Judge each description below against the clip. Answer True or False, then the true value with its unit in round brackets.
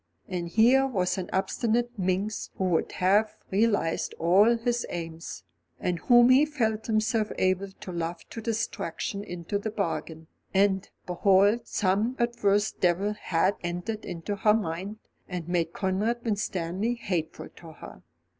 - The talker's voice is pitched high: True (200 Hz)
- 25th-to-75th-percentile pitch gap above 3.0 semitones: True (3.7 semitones)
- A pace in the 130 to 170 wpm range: True (140 wpm)